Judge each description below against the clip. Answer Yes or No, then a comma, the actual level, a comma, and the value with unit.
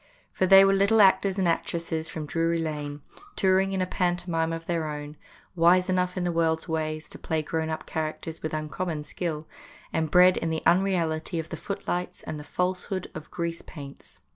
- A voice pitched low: No, medium, 165 Hz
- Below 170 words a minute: No, average, 190 wpm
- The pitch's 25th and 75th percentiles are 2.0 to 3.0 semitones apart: Yes, narrow, 2.6 semitones